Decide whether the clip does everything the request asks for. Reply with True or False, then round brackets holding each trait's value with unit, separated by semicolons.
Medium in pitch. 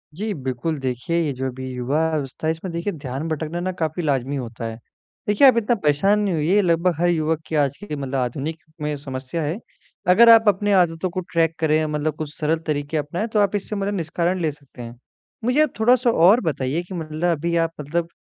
True (160 Hz)